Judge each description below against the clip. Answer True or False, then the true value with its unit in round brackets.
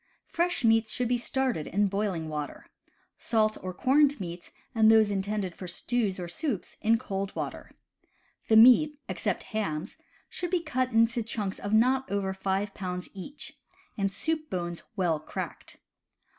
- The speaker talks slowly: False (155 wpm)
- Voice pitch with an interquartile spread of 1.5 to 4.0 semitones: False (4.5 semitones)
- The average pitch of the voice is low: False (215 Hz)